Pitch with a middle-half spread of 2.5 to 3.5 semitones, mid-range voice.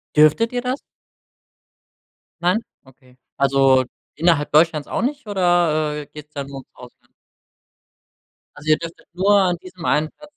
No: average, 4.1 semitones; medium, 155 Hz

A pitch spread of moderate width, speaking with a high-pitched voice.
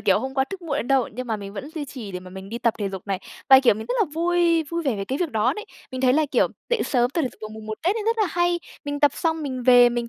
No: wide, 6.9 semitones; very high, 260 Hz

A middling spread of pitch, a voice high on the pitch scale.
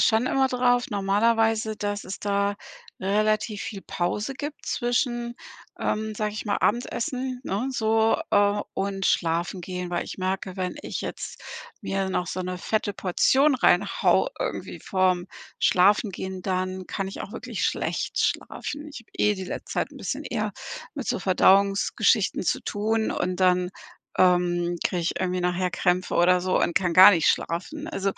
Yes: average, 3.3 semitones; high, 200 Hz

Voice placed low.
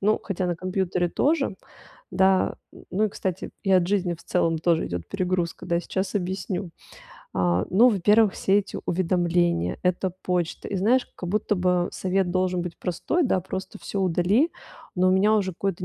No: medium, 185 Hz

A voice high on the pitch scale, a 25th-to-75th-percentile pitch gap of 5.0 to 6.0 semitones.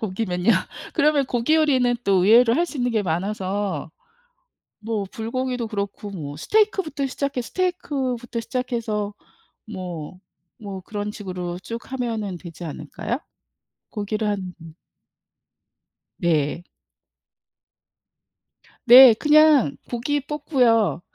Yes: high, 225 Hz; wide, 5.4 semitones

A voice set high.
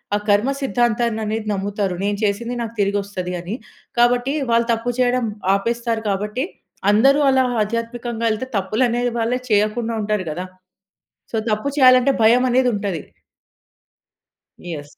Yes: high, 230 Hz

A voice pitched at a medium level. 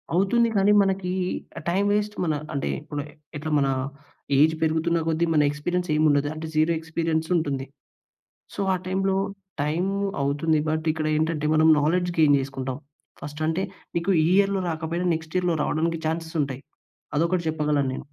Yes: medium, 160 Hz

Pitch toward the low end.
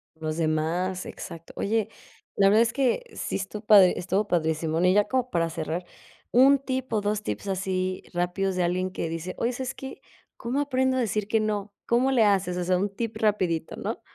No: high, 200 Hz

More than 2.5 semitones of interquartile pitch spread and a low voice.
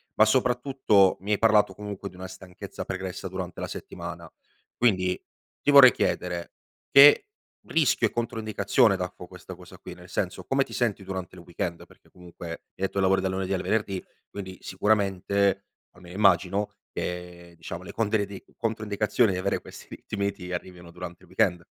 Yes: average, 2.9 semitones; very low, 95 Hz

